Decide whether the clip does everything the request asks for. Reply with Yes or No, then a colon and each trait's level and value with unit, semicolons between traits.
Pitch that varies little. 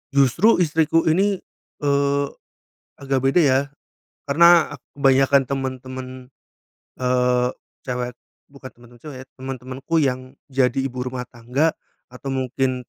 Yes: narrow, 1.9 semitones